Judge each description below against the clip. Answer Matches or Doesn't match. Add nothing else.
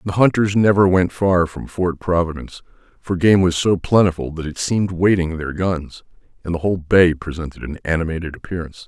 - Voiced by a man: Matches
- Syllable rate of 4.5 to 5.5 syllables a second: Doesn't match